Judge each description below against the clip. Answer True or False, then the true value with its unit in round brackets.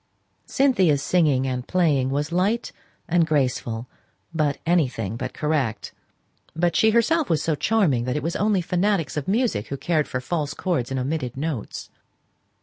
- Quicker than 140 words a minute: True (155 wpm)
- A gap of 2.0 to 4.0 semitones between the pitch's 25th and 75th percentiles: False (5.5 semitones)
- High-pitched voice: False (155 Hz)